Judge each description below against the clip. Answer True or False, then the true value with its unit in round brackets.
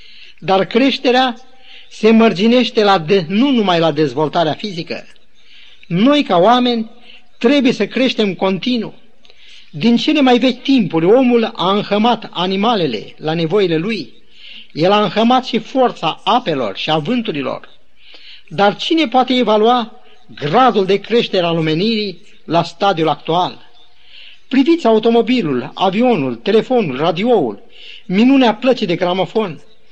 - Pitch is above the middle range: True (220 Hz)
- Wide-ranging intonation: False (4.8 semitones)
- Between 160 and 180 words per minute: False (120 wpm)